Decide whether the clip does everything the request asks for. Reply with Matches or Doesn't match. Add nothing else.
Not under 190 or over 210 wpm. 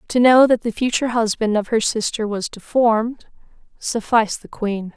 Doesn't match